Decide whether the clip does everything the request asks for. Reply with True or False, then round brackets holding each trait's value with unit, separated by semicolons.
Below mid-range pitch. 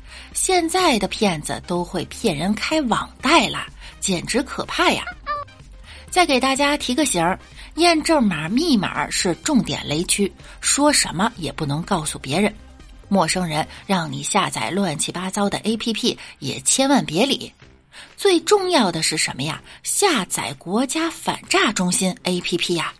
False (205 Hz)